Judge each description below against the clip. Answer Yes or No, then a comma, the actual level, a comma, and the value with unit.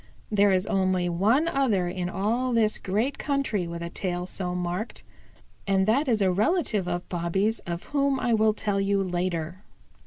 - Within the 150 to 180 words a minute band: Yes, average, 175 wpm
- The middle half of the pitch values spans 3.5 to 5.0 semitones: Yes, average, 4.0 semitones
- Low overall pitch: No, high, 195 Hz